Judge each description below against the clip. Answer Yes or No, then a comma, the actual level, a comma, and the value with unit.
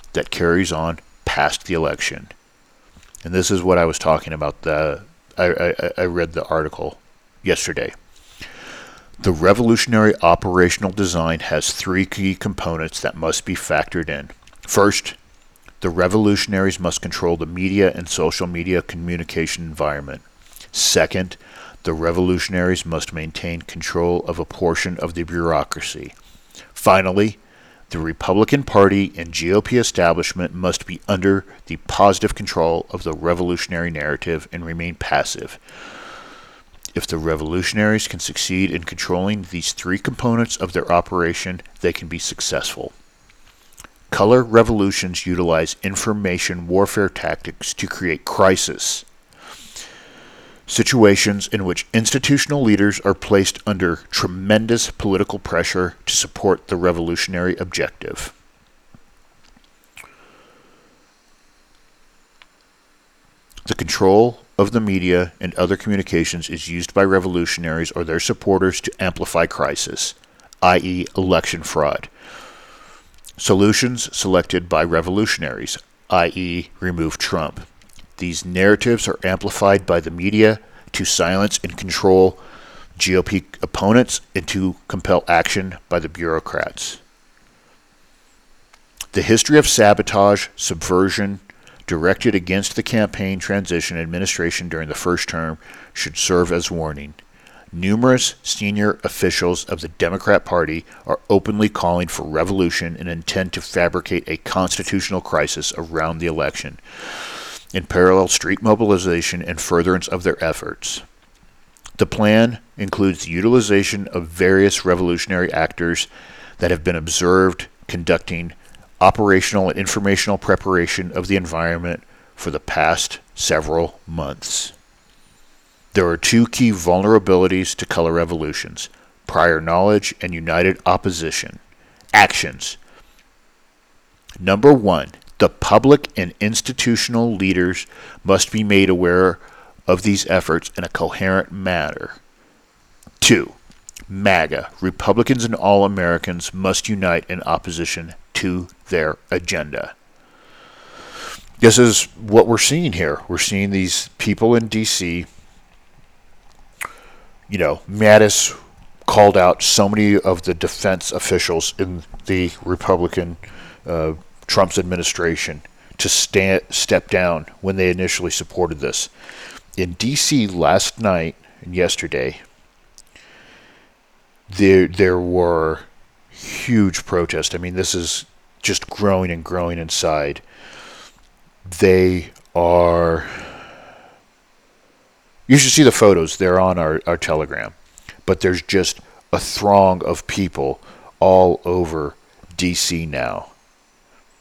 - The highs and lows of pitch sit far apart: No, average, 2.8 semitones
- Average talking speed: No, slow, 115 wpm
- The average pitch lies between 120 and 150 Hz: No, very low, 90 Hz